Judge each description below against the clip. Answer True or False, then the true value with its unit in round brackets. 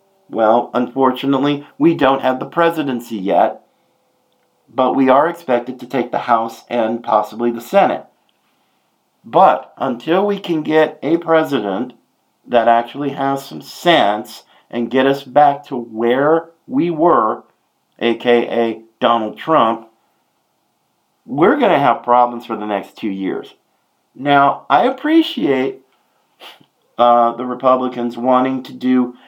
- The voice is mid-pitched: False (130 Hz)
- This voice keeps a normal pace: False (125 wpm)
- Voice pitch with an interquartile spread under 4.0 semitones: True (3.3 semitones)